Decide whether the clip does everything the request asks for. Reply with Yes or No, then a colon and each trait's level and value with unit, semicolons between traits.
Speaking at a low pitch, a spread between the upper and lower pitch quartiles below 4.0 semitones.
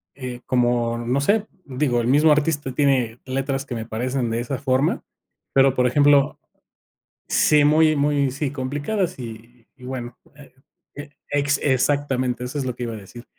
Yes: low, 130 Hz; average, 2.8 semitones